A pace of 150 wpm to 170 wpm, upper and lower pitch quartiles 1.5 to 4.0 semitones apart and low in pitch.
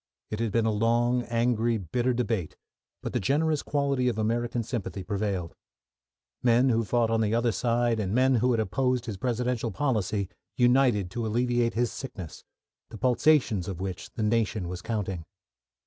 Yes: average, 165 wpm; average, 2.8 semitones; low, 115 Hz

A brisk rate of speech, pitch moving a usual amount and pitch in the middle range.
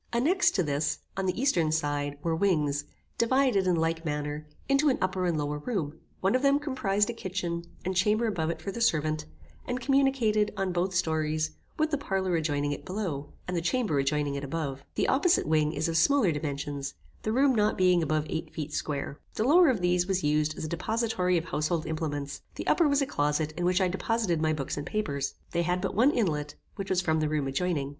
No: fast, 215 wpm; wide, 5.8 semitones; medium, 175 Hz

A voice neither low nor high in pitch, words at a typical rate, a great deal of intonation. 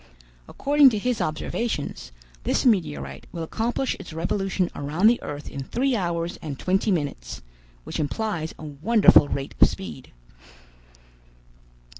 No: medium, 170 Hz; slow, 130 wpm; wide, 7.1 semitones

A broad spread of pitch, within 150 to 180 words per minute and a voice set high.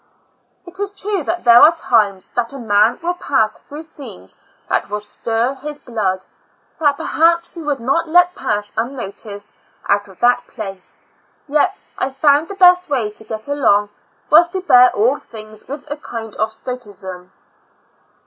Yes: wide, 6.3 semitones; average, 165 wpm; high, 245 Hz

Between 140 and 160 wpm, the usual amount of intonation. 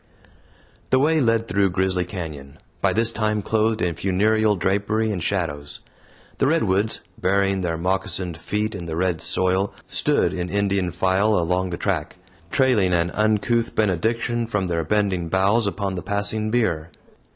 Yes: average, 150 wpm; average, 3.4 semitones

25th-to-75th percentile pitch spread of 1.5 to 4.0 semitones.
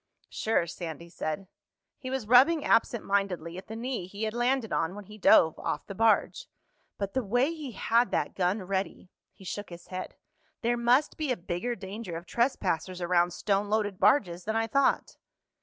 No: average, 4.8 semitones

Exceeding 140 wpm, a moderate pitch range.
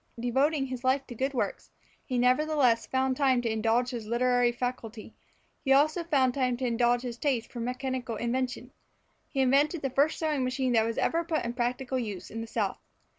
No: average, 190 wpm; narrow, 2.1 semitones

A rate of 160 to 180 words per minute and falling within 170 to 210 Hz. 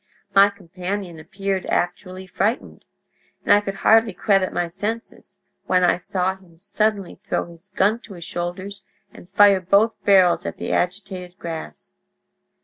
No: average, 145 wpm; high, 190 Hz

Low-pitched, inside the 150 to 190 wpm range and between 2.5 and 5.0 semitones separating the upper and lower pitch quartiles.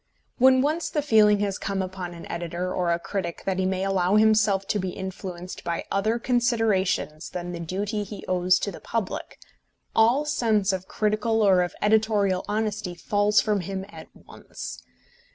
No: high, 195 Hz; average, 170 wpm; average, 2.9 semitones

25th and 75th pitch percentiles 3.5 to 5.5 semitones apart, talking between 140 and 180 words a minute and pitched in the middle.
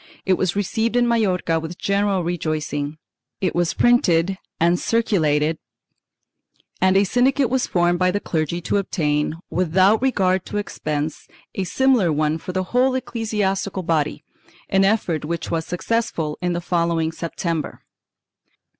Yes: average, 3.9 semitones; average, 145 wpm; medium, 180 Hz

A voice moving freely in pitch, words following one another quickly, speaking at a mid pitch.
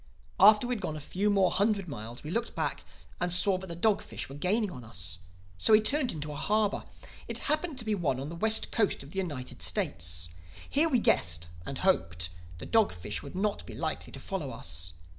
Yes: wide, 8.5 semitones; fast, 220 wpm; medium, 180 Hz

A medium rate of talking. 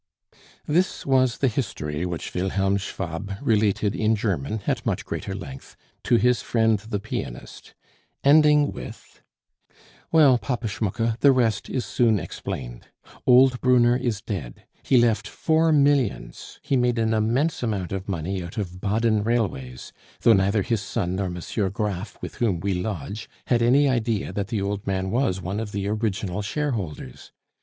Yes: average, 155 wpm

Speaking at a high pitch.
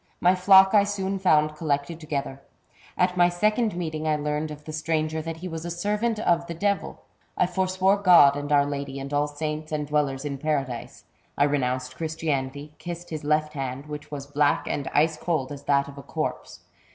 No: medium, 155 Hz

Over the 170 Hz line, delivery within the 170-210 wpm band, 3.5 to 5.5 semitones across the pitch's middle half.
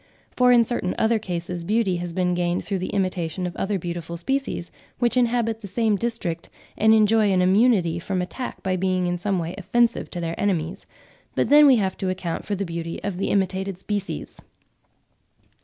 Yes: high, 190 Hz; average, 190 wpm; average, 3.8 semitones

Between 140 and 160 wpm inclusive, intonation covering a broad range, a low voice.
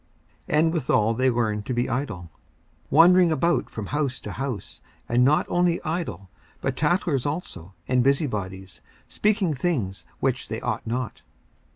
Yes: average, 150 wpm; wide, 6.9 semitones; low, 130 Hz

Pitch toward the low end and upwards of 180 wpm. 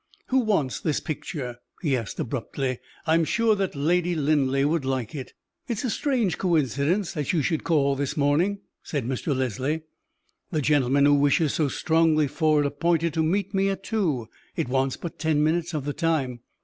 No: medium, 155 Hz; average, 190 wpm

